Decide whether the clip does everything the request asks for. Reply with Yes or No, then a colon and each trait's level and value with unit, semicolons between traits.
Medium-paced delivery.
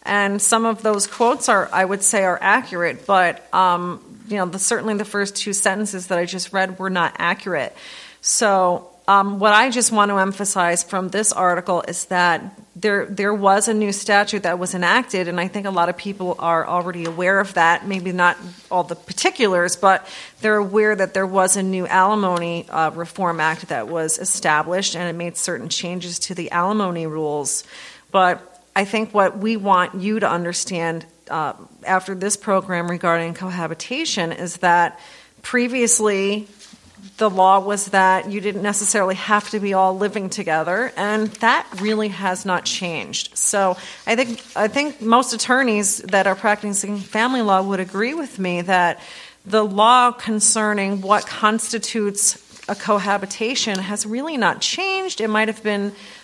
Yes: average, 170 wpm